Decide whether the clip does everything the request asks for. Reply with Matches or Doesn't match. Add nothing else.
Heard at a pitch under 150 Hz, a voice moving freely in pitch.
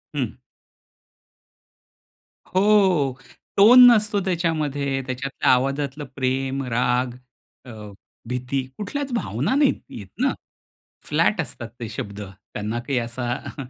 Matches